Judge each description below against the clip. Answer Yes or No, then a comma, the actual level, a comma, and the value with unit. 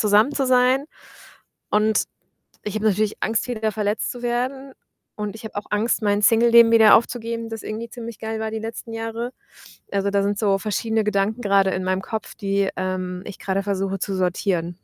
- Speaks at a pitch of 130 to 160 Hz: No, high, 215 Hz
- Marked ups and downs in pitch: No, narrow, 2.5 semitones